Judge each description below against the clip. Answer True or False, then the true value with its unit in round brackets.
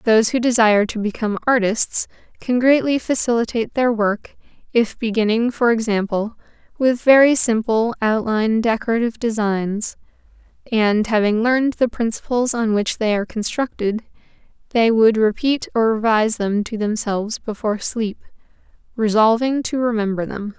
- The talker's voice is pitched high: True (225 Hz)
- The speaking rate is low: True (130 wpm)